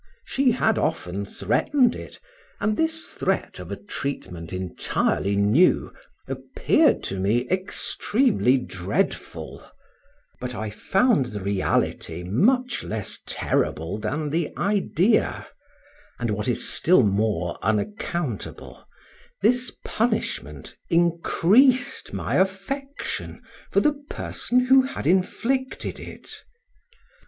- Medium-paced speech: No, slow, 105 wpm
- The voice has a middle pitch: Yes, medium, 165 Hz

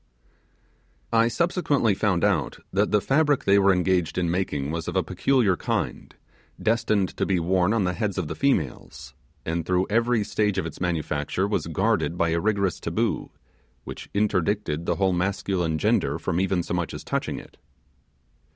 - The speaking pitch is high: No, very low, 95 Hz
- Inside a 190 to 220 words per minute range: No, average, 170 wpm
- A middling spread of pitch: Yes, average, 3.4 semitones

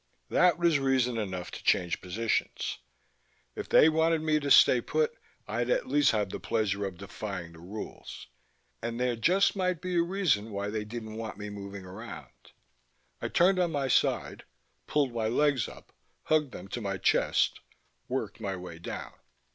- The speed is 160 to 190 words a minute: Yes, average, 170 wpm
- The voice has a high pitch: No, low, 115 Hz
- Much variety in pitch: Yes, wide, 7.4 semitones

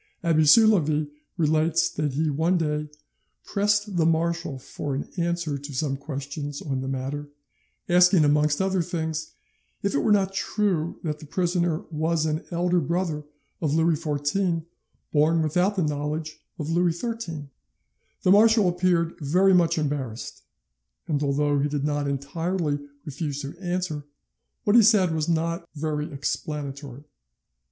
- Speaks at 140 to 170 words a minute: Yes, average, 145 wpm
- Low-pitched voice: No, medium, 160 Hz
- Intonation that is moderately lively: Yes, average, 3.2 semitones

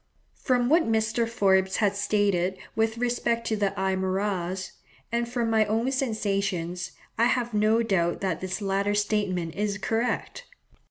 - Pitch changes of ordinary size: Yes, average, 3.3 semitones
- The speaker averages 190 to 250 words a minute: No, average, 145 wpm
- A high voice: Yes, high, 210 Hz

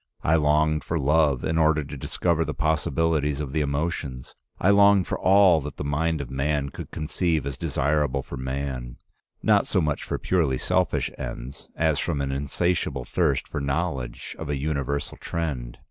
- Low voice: Yes, very low, 75 Hz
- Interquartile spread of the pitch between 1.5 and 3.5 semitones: Yes, average, 2.8 semitones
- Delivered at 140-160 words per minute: No, average, 175 wpm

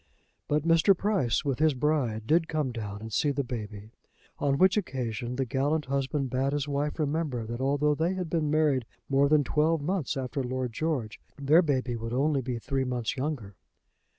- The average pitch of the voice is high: No, medium, 140 Hz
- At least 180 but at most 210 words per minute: Yes, average, 185 wpm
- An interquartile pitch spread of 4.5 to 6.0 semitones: No, average, 3.7 semitones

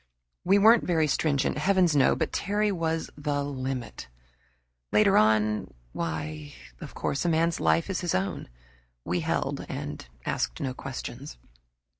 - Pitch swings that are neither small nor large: No, wide, 8.3 semitones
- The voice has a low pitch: No, medium, 145 Hz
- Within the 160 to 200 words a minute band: No, average, 140 wpm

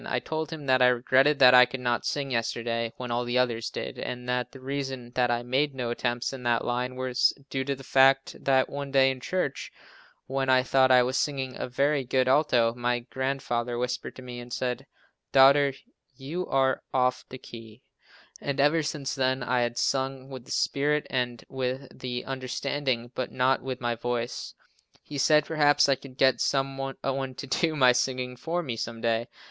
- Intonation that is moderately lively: No, narrow, 1.8 semitones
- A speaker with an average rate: Yes, average, 195 wpm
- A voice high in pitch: No, low, 130 Hz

